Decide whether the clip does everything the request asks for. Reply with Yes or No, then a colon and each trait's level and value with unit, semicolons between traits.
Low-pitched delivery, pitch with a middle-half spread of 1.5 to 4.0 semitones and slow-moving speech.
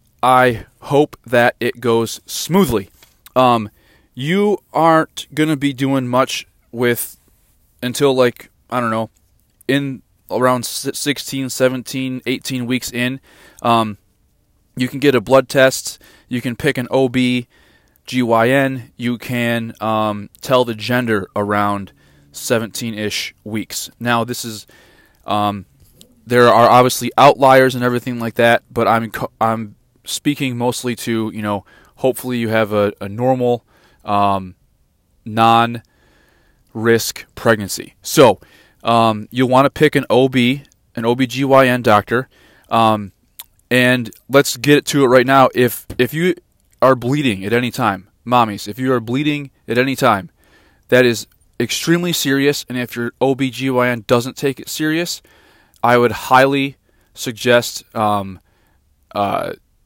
Yes: low, 120 Hz; average, 3.1 semitones; slow, 130 wpm